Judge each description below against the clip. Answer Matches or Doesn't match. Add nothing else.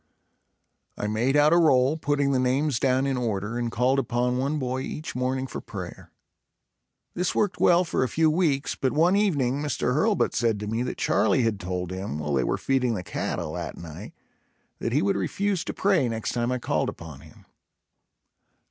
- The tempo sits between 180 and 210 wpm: Matches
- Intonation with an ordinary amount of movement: Matches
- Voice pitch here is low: Matches